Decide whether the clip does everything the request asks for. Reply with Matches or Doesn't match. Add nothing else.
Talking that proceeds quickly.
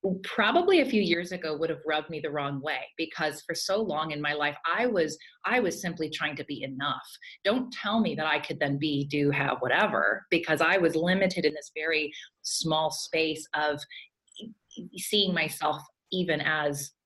Doesn't match